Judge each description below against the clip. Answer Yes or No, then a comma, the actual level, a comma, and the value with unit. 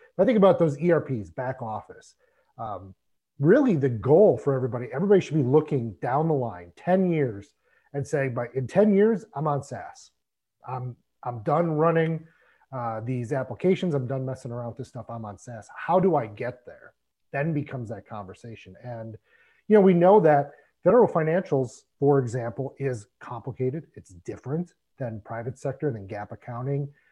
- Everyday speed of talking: Yes, average, 170 wpm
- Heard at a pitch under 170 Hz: Yes, low, 135 Hz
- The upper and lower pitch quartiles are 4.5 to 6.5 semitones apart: Yes, average, 5.0 semitones